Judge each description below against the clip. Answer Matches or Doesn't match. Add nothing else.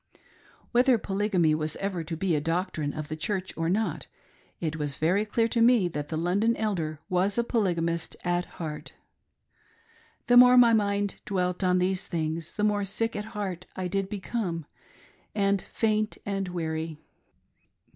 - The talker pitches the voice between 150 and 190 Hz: Matches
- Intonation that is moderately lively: Matches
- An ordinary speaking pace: Matches